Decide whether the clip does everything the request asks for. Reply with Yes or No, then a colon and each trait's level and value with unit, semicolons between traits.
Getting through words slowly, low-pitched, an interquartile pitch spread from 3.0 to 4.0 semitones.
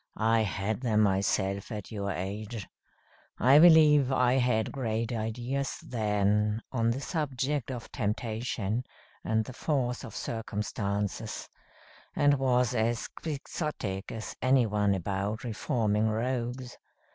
Yes: slow, 120 wpm; low, 115 Hz; average, 3.4 semitones